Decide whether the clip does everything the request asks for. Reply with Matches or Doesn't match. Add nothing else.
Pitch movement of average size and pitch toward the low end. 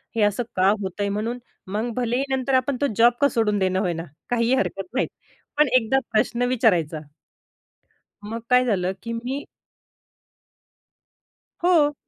Doesn't match